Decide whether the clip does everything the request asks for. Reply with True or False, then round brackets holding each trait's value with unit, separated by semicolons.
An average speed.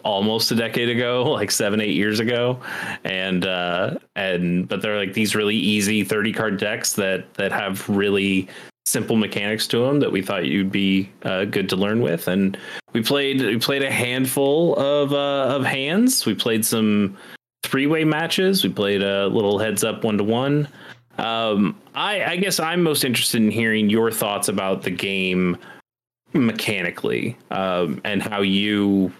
True (175 wpm)